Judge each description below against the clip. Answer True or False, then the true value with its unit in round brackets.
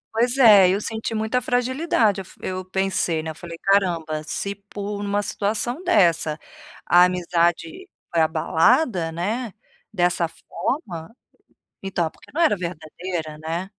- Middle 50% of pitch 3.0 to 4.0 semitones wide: False (4.5 semitones)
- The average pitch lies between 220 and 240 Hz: False (190 Hz)